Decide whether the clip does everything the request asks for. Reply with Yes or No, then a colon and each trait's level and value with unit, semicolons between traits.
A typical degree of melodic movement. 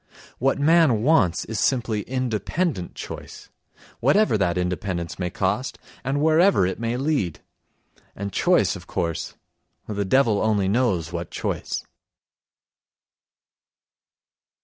No: wide, 6.4 semitones